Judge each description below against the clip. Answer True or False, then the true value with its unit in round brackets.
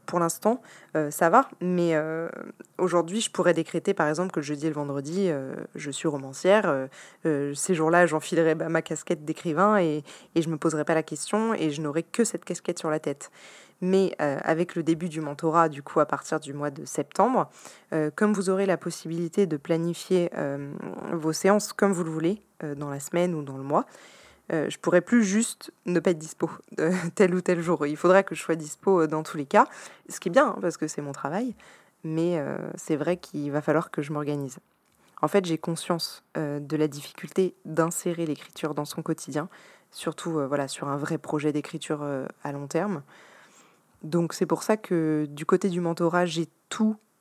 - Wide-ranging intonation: False (2.9 semitones)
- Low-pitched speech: False (165 Hz)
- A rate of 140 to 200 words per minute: False (210 wpm)